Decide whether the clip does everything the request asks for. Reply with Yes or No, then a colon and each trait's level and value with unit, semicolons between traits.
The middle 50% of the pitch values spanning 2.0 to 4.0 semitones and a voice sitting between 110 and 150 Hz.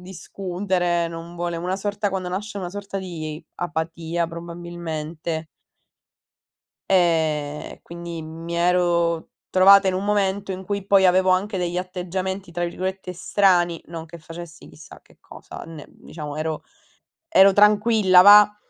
No: narrow, 2.4 semitones; medium, 175 Hz